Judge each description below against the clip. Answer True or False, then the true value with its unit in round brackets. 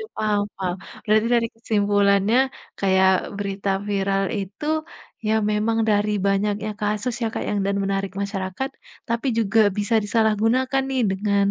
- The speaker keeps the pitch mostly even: True (2.1 semitones)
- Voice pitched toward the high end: True (205 Hz)